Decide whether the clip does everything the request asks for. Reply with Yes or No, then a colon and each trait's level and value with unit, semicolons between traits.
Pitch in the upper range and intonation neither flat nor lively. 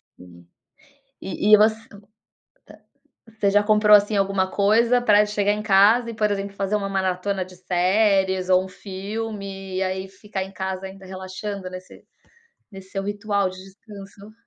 No: high, 195 Hz; narrow, 1.8 semitones